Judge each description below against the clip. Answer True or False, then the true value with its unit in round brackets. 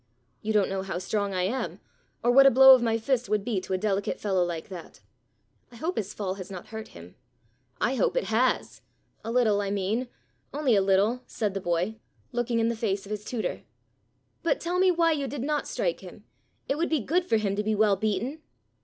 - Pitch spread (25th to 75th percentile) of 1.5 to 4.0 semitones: False (4.7 semitones)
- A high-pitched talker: True (220 Hz)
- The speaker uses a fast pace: True (225 wpm)